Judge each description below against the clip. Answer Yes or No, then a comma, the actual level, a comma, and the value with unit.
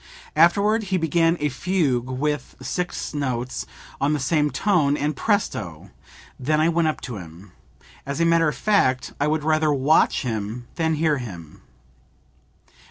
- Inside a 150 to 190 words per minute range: Yes, average, 155 wpm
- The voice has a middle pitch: Yes, medium, 150 Hz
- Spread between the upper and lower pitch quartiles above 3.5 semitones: Yes, average, 4.5 semitones